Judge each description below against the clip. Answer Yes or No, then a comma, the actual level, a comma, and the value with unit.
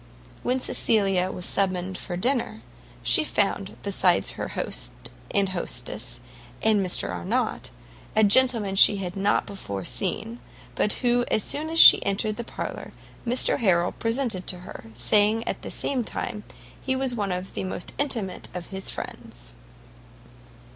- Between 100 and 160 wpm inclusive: Yes, average, 150 wpm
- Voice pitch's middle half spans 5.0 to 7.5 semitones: No, average, 4.3 semitones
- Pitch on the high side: Yes, high, 200 Hz